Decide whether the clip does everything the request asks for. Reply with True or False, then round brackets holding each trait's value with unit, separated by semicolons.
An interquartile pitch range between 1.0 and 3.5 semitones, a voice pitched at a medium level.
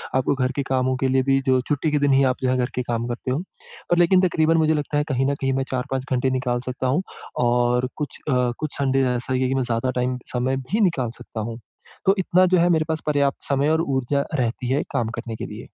False (2.7 semitones; 130 Hz)